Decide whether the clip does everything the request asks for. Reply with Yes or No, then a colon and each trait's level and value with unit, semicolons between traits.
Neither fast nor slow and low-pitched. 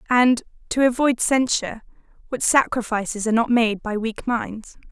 No: average, 145 wpm; high, 235 Hz